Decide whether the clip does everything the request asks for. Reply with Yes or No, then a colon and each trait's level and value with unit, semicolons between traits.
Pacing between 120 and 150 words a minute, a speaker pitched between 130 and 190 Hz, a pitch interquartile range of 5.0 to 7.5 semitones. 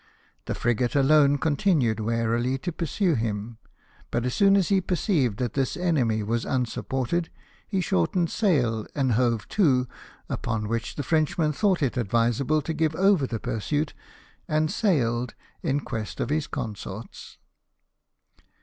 Yes: average, 140 wpm; low, 135 Hz; wide, 5.6 semitones